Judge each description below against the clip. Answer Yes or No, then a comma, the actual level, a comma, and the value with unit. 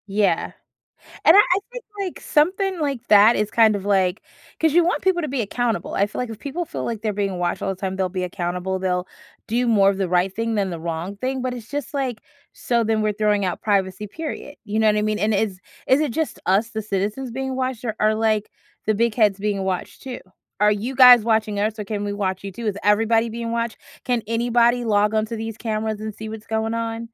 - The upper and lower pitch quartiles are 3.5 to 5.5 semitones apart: No, average, 3.0 semitones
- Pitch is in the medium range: No, high, 220 Hz